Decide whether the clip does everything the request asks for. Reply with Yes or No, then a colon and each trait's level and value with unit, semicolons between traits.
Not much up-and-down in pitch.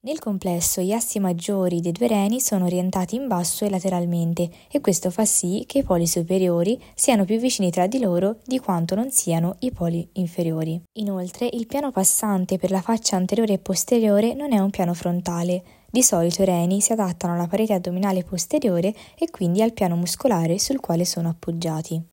No: average, 3.8 semitones